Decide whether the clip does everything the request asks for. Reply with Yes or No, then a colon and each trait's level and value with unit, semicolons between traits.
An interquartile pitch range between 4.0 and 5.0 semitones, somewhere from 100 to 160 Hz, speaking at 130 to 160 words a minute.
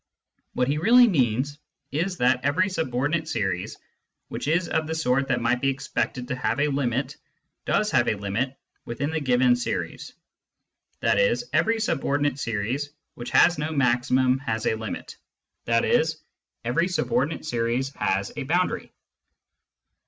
Yes: average, 4.3 semitones; low, 135 Hz; average, 145 wpm